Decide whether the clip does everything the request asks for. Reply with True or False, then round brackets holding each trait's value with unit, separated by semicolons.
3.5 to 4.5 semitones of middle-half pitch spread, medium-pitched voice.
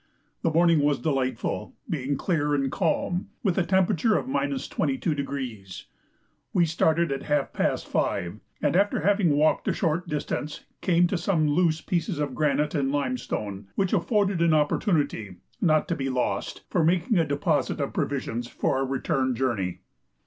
True (4.2 semitones; 150 Hz)